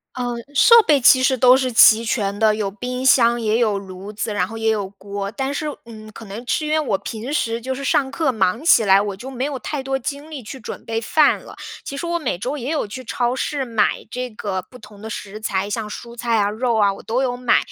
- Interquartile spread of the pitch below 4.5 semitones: Yes, average, 4.0 semitones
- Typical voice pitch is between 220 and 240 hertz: Yes, high, 235 Hz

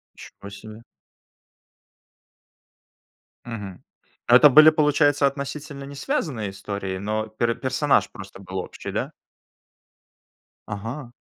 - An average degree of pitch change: No, wide, 5.8 semitones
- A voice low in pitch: Yes, low, 120 Hz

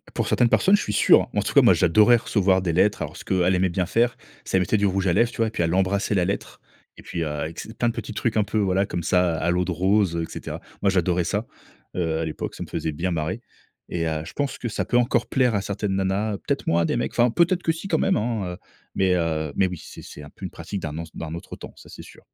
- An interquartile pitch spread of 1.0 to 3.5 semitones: No, average, 4.4 semitones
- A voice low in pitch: Yes, very low, 95 Hz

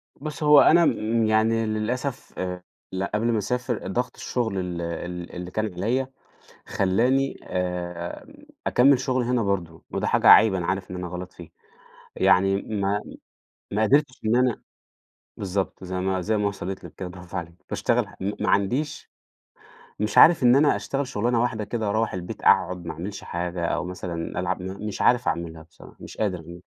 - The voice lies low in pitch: Yes, low, 100 Hz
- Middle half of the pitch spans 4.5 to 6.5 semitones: Yes, average, 4.9 semitones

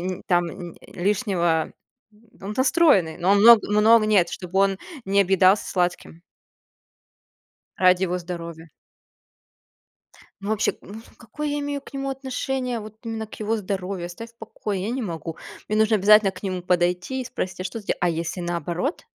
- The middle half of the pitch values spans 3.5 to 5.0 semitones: Yes, average, 4.0 semitones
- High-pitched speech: Yes, high, 195 Hz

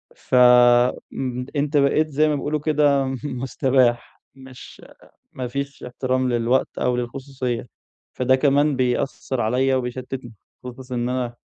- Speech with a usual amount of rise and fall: No, narrow, 2.0 semitones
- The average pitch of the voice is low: Yes, low, 130 Hz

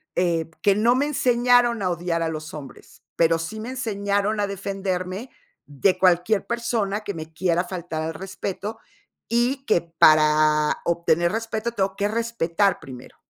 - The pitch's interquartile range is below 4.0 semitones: No, average, 4.8 semitones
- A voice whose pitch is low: No, high, 190 Hz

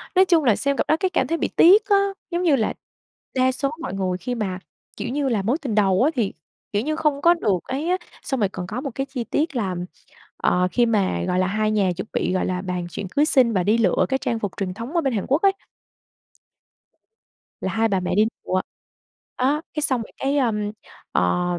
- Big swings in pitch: Yes, wide, 6.6 semitones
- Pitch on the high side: Yes, high, 235 Hz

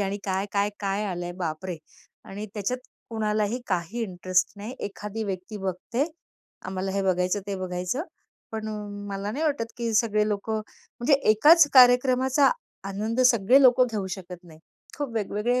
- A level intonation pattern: No, average, 3.7 semitones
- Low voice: No, high, 210 Hz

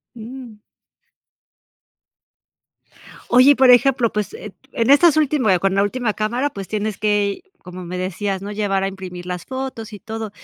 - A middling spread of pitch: Yes, average, 4.3 semitones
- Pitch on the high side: Yes, high, 215 Hz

